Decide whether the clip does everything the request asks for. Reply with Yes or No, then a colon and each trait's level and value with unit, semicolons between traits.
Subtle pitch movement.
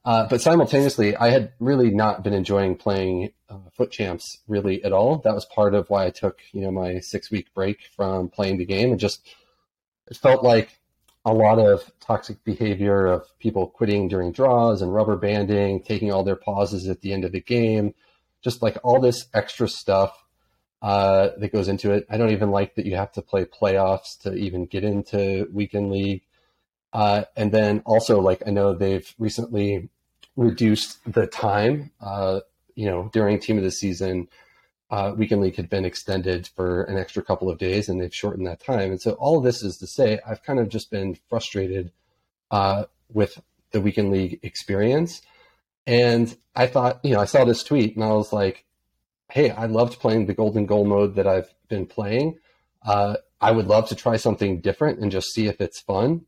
Yes: narrow, 2.3 semitones